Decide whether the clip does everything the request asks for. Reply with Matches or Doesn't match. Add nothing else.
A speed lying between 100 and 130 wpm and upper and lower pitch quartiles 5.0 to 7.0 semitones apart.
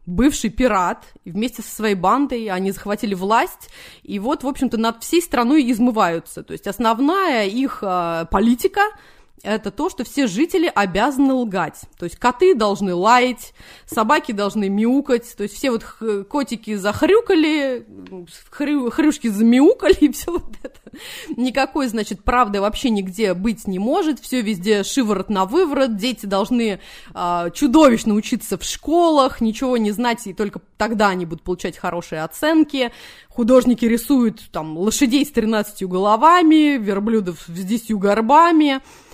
Doesn't match